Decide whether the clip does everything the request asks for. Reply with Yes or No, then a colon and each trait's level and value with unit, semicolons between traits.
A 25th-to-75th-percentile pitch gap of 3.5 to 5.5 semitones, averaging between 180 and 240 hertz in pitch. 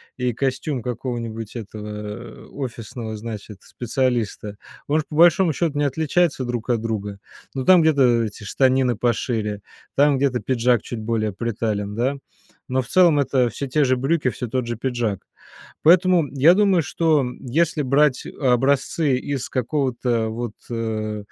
No: average, 3.9 semitones; low, 125 Hz